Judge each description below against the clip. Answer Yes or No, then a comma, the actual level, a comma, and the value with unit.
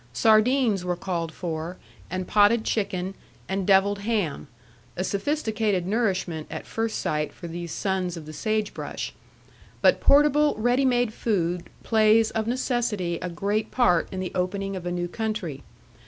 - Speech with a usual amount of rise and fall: Yes, average, 3.9 semitones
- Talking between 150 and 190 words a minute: Yes, average, 155 wpm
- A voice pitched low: No, high, 195 Hz